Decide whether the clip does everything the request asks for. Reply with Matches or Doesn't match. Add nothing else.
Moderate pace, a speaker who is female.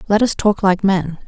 Doesn't match